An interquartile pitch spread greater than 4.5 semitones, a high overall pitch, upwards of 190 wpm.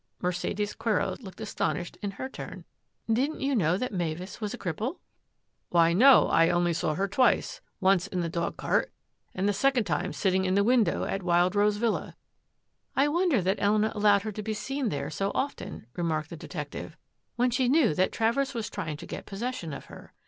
Yes: average, 5.3 semitones; high, 205 Hz; fast, 205 wpm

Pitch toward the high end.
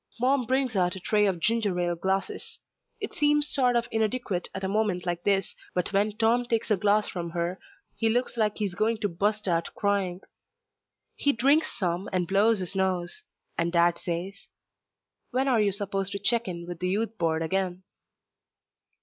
Yes: high, 200 Hz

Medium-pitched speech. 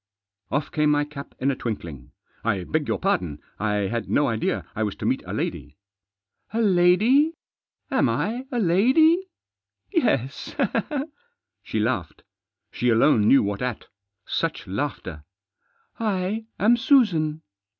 Yes: medium, 155 Hz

